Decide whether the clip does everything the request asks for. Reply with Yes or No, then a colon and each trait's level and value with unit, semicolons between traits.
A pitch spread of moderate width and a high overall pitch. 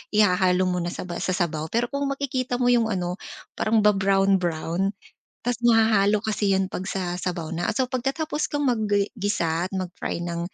Yes: average, 4.5 semitones; high, 195 Hz